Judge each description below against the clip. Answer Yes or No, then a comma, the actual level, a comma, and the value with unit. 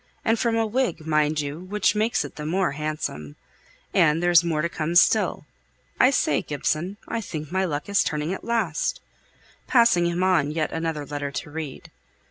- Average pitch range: Yes, average, 4.1 semitones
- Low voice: No, medium, 165 Hz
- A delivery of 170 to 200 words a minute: Yes, average, 180 wpm